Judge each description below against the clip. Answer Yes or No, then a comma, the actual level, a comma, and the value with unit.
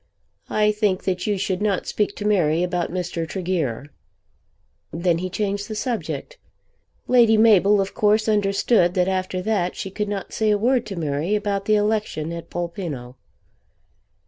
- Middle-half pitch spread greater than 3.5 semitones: No, average, 3.2 semitones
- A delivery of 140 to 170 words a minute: Yes, average, 160 wpm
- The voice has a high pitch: Yes, high, 195 Hz